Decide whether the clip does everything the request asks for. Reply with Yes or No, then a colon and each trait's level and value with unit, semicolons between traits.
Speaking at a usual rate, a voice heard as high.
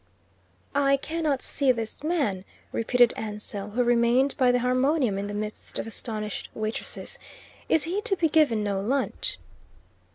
Yes: average, 150 wpm; high, 245 Hz